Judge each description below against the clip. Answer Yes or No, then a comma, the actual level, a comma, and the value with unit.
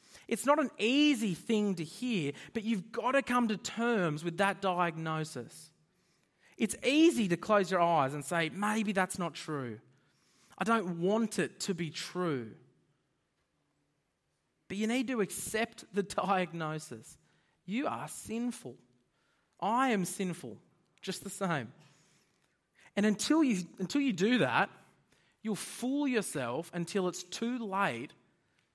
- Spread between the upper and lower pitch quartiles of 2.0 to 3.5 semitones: No, average, 5.1 semitones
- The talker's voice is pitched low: No, high, 190 Hz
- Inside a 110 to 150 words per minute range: Yes, average, 140 wpm